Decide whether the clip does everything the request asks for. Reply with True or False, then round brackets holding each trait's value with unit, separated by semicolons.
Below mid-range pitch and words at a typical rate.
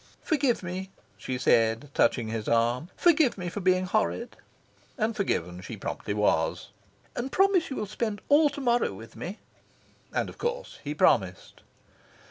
False (190 Hz; 155 wpm)